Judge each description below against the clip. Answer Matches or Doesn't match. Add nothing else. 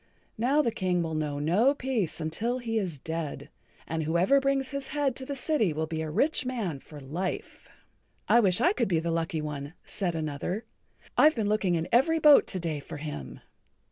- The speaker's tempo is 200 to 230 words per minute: Matches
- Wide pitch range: Matches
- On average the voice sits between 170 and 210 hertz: Matches